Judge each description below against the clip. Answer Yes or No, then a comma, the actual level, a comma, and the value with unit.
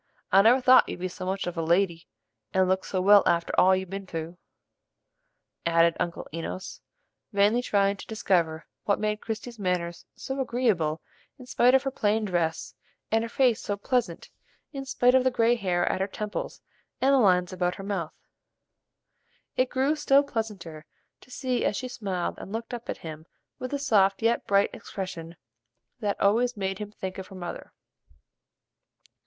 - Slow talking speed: No, average, 175 wpm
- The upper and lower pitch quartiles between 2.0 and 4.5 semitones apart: No, average, 4.9 semitones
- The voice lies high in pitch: Yes, high, 200 Hz